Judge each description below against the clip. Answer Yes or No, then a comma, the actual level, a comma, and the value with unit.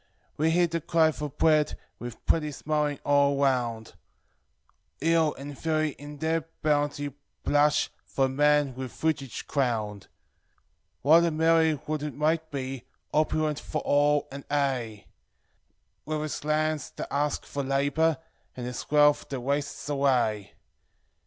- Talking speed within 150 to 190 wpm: No, average, 140 wpm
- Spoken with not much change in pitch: Yes, narrow, 2.2 semitones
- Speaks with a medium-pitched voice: Yes, medium, 145 Hz